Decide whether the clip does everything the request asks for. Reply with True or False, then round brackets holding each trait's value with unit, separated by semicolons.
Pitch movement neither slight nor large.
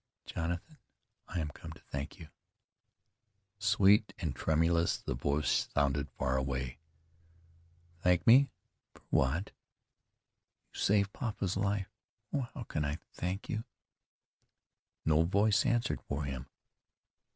False (6.1 semitones)